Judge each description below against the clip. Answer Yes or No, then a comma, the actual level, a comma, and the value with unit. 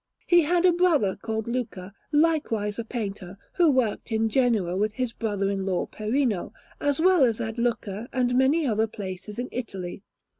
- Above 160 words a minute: Yes, average, 175 wpm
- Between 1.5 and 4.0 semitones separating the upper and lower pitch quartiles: No, average, 4.4 semitones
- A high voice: Yes, high, 225 Hz